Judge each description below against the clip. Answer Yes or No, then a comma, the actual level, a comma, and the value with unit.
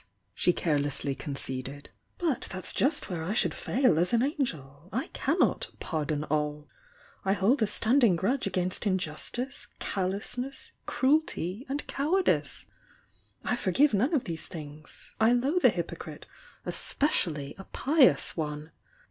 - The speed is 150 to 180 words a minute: No, average, 140 wpm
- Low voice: No, high, 195 Hz